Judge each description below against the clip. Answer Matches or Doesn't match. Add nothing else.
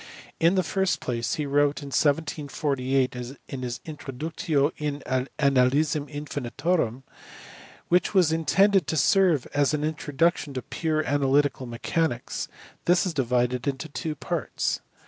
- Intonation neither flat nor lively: Matches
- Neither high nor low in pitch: Matches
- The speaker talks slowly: Matches